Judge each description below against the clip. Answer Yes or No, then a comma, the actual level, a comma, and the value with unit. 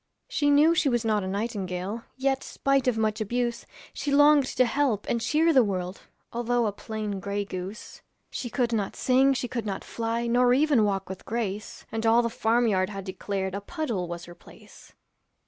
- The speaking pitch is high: Yes, high, 225 Hz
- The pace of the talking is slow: No, average, 190 wpm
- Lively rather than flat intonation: No, average, 4.0 semitones